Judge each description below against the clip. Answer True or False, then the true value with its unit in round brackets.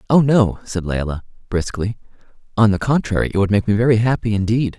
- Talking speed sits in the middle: True (190 wpm)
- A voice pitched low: True (105 Hz)